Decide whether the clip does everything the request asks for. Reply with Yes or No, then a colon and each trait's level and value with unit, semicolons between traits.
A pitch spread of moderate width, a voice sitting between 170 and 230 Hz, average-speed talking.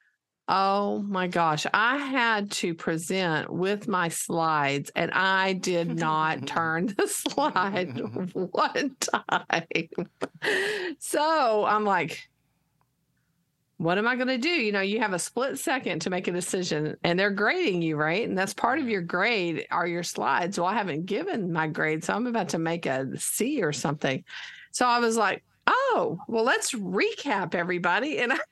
No: wide, 6.0 semitones; high, 190 Hz; average, 165 wpm